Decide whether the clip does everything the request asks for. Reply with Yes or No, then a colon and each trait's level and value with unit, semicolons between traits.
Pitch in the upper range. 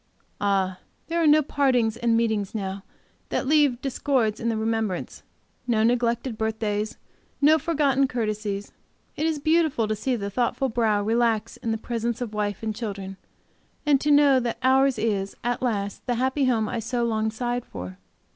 Yes: high, 230 Hz